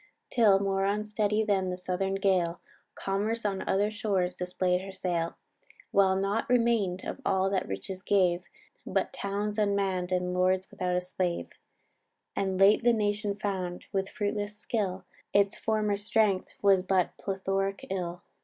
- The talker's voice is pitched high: Yes, high, 195 Hz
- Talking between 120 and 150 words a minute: Yes, average, 145 wpm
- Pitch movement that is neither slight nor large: No, narrow, 1.9 semitones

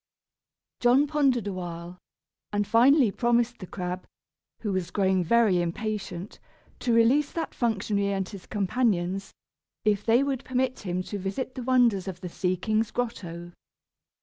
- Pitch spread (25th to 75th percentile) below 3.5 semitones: No, average, 4.7 semitones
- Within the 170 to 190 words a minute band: No, average, 145 wpm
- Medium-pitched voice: No, high, 205 Hz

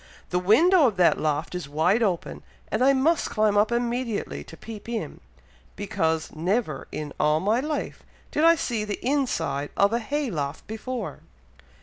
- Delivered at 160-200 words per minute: Yes, average, 165 wpm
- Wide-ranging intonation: Yes, wide, 7.4 semitones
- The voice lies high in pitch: Yes, high, 210 Hz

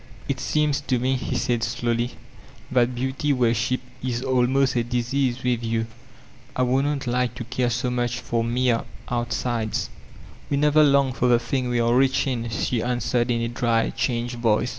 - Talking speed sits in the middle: Yes, average, 180 wpm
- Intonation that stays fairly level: Yes, narrow, 1.6 semitones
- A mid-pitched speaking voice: No, low, 125 Hz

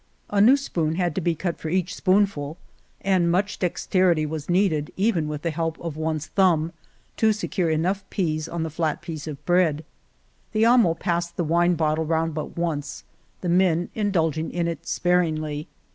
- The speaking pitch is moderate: Yes, medium, 170 Hz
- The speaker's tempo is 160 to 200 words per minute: Yes, average, 180 wpm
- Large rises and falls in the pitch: No, average, 2.8 semitones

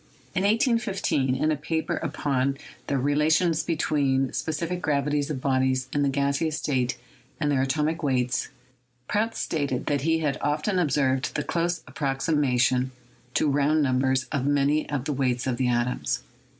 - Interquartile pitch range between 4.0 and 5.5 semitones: No, average, 3.0 semitones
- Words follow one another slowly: No, average, 165 wpm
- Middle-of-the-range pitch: Yes, medium, 145 Hz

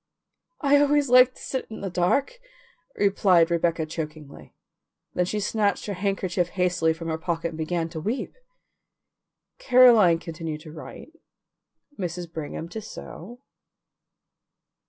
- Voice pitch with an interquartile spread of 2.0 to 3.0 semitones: No, average, 4.8 semitones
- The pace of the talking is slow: Yes, slow, 130 wpm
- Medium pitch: Yes, medium, 180 Hz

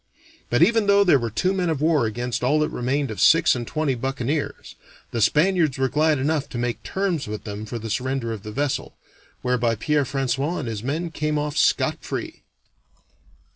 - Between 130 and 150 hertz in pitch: Yes, low, 135 Hz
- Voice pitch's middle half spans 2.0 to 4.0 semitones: No, average, 4.6 semitones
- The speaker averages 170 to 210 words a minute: Yes, average, 195 wpm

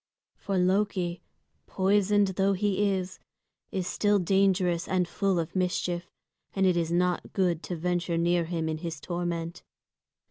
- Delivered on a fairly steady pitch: Yes, narrow, 2.0 semitones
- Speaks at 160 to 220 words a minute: No, average, 145 wpm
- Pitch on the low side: No, medium, 180 Hz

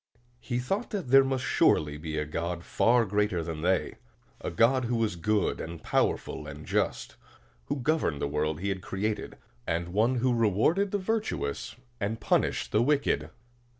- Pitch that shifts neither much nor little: No, wide, 7.2 semitones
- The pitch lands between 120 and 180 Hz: No, low, 105 Hz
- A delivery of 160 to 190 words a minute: Yes, average, 165 wpm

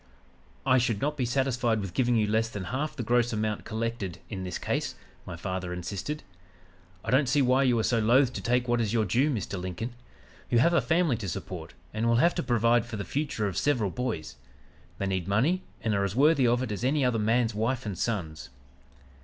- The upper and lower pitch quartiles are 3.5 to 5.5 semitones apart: Yes, average, 4.1 semitones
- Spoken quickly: Yes, fast, 220 wpm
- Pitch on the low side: Yes, low, 115 Hz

